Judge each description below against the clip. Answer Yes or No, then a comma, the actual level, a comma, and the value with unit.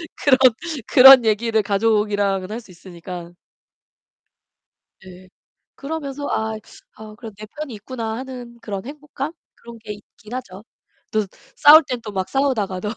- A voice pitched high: Yes, high, 220 Hz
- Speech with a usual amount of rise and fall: Yes, average, 4.4 semitones